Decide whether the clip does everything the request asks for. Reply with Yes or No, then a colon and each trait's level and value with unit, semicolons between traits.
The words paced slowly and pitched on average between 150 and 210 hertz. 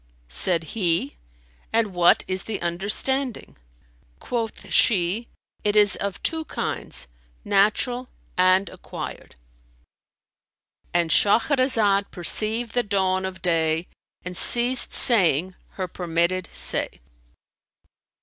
Yes: slow, 95 wpm; high, 190 Hz